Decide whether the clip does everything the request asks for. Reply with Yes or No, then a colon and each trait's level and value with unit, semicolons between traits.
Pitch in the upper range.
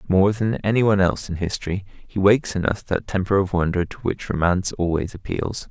No: very low, 95 Hz